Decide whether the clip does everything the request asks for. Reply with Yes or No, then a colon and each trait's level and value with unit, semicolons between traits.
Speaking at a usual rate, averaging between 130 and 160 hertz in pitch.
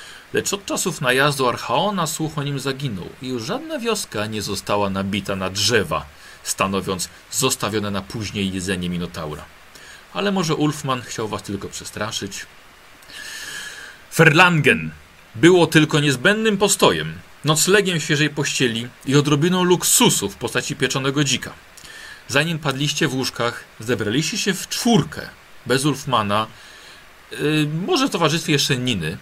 Yes: average, 125 wpm; low, 135 Hz